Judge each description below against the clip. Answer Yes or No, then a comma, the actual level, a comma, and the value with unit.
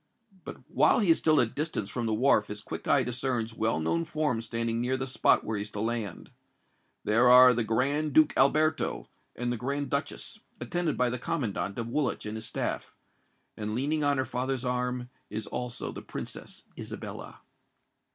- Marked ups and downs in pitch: No, average, 3.8 semitones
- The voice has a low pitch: Yes, low, 125 Hz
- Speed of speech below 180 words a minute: No, average, 190 wpm